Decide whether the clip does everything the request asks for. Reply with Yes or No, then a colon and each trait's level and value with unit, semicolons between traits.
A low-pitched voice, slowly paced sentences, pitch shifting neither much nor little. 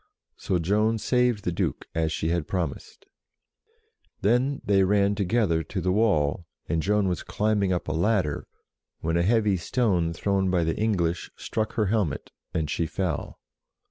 No: very low, 95 Hz; average, 160 wpm; average, 4.2 semitones